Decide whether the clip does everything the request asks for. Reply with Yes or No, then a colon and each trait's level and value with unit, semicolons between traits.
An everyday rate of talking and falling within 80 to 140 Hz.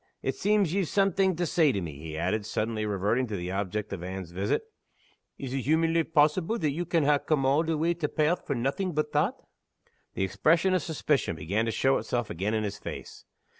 No: fast, 210 wpm; low, 135 Hz